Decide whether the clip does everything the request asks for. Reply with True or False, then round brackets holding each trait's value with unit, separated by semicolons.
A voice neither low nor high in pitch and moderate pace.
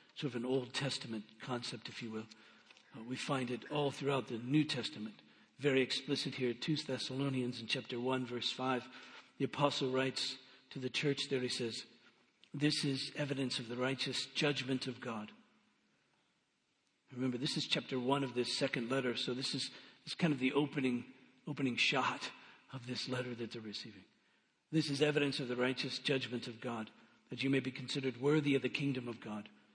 False (130 Hz; 185 wpm)